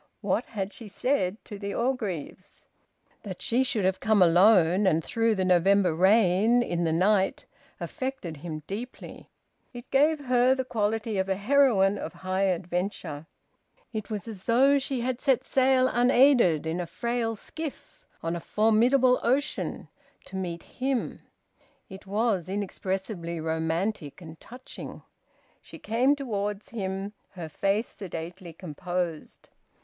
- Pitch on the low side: No, high, 200 Hz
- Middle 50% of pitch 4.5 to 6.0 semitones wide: Yes, average, 5.1 semitones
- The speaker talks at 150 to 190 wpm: No, average, 140 wpm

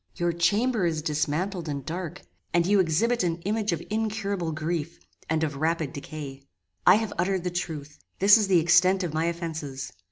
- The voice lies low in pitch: No, medium, 170 Hz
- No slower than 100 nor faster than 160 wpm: No, average, 180 wpm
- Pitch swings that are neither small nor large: Yes, average, 3.7 semitones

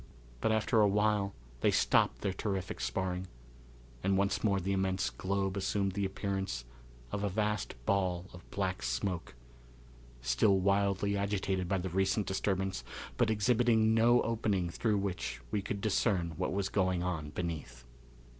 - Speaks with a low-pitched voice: Yes, very low, 95 Hz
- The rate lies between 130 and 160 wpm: Yes, average, 150 wpm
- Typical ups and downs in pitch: No, narrow, 1.9 semitones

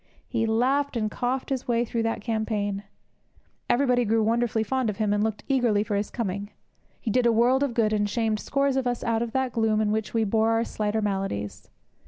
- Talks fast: Yes, fast, 215 wpm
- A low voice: No, high, 225 Hz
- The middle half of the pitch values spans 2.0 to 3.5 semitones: Yes, narrow, 2.5 semitones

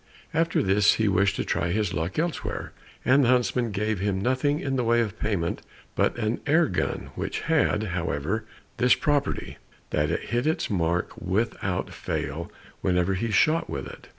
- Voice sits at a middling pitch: No, low, 105 Hz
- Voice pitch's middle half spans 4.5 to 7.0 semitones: Yes, wide, 5.4 semitones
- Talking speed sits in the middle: Yes, average, 175 wpm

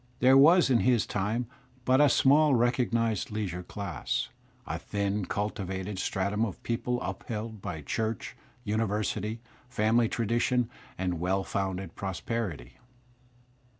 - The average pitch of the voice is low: Yes, low, 110 Hz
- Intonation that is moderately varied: Yes, average, 3.7 semitones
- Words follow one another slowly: Yes, slow, 115 wpm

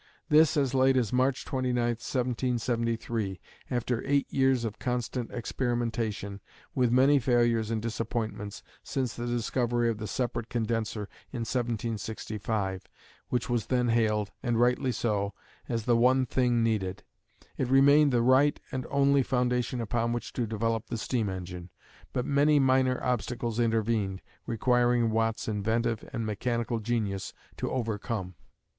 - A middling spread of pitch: No, narrow, 2.2 semitones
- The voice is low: Yes, low, 120 Hz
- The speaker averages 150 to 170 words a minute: No, average, 140 wpm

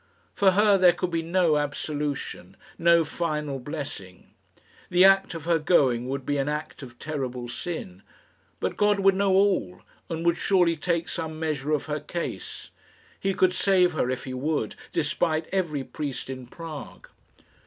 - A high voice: No, medium, 155 Hz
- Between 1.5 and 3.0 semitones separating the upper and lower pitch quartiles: No, average, 4.2 semitones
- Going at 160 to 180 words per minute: Yes, average, 165 wpm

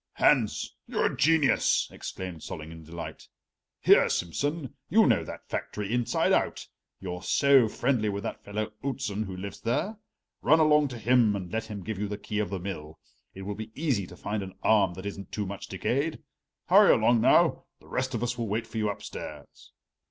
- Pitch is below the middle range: Yes, low, 105 Hz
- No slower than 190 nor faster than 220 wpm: Yes, average, 195 wpm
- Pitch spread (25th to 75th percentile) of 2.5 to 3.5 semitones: No, average, 4.2 semitones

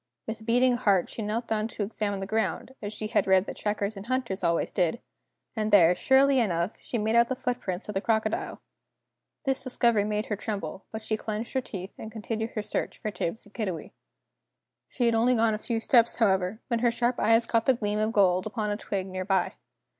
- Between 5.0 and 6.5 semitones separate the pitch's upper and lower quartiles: No, average, 2.7 semitones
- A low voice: No, high, 215 Hz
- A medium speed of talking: No, fast, 215 wpm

